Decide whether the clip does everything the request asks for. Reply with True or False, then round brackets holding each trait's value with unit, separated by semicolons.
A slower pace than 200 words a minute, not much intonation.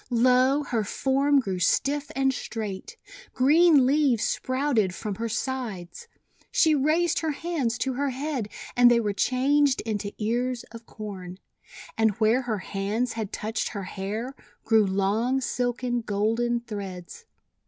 False (140 wpm; 4.1 semitones)